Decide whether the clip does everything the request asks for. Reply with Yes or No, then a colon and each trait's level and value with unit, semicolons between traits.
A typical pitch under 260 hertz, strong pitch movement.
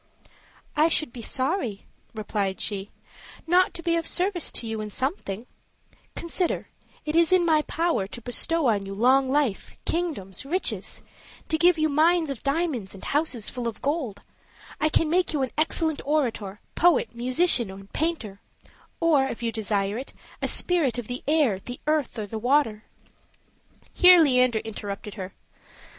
No: very high, 270 Hz; wide, 6.9 semitones